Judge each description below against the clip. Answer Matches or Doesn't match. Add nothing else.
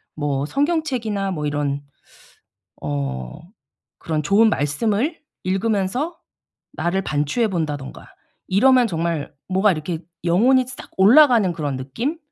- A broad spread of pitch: Matches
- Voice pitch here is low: Doesn't match